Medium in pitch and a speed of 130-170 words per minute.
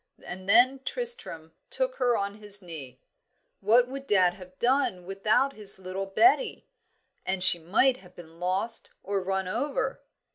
No: high, 195 Hz; average, 150 wpm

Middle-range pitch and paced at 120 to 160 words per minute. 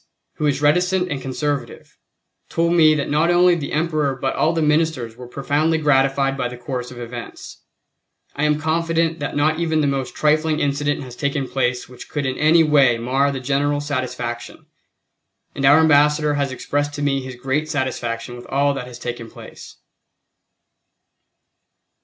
No: medium, 145 Hz; average, 170 wpm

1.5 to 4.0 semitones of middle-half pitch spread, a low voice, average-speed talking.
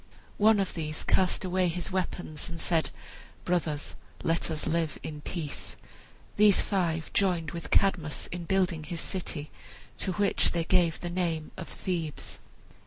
No: narrow, 2.5 semitones; medium, 170 Hz; average, 150 wpm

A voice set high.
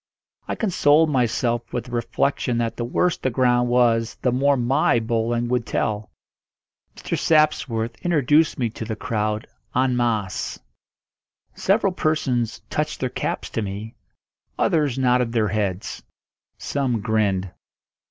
No: low, 120 Hz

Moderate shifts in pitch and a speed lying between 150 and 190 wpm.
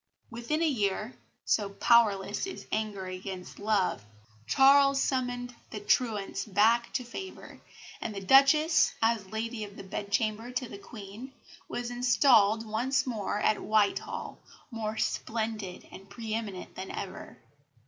No: average, 3.4 semitones; slow, 135 wpm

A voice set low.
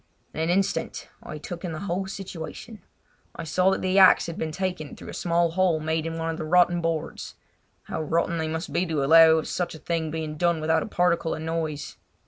No: medium, 165 Hz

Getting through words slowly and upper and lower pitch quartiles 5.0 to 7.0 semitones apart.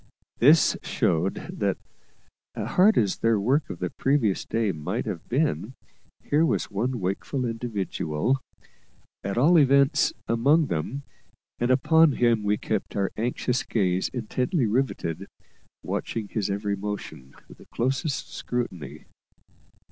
Yes: slow, 125 wpm; wide, 5.5 semitones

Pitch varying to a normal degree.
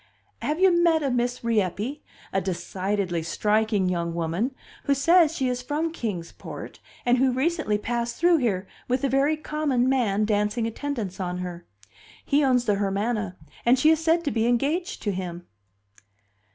No: wide, 6.4 semitones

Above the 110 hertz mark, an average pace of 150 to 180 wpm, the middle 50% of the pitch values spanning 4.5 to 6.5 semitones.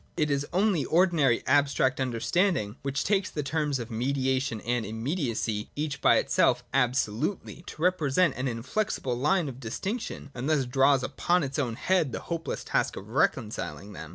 Yes: low, 135 Hz; average, 160 wpm; average, 4.8 semitones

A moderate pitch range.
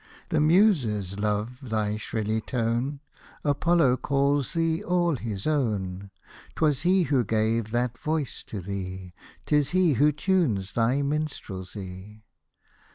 No: wide, 6.3 semitones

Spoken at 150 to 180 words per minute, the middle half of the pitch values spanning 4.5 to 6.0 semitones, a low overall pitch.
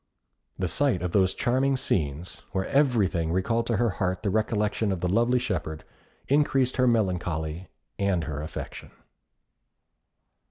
No: slow, 135 wpm; average, 5.3 semitones; very low, 95 Hz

